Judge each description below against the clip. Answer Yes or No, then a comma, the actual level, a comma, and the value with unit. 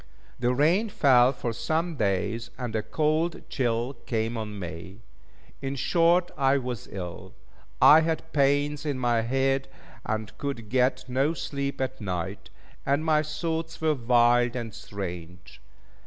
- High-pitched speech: No, low, 130 Hz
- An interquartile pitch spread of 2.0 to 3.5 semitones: No, average, 5.0 semitones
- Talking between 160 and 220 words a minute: No, average, 140 wpm